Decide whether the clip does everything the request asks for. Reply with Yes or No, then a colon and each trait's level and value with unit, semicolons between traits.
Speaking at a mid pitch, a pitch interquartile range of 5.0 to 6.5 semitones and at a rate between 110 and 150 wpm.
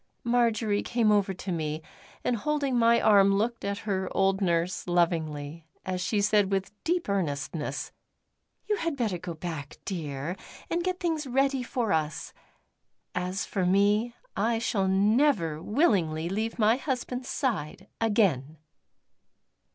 No: high, 200 Hz; wide, 5.5 semitones; slow, 135 wpm